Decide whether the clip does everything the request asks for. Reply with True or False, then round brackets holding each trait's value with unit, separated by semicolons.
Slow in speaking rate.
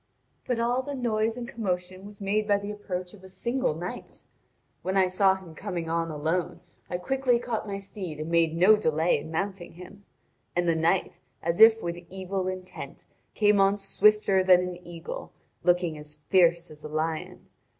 False (180 wpm)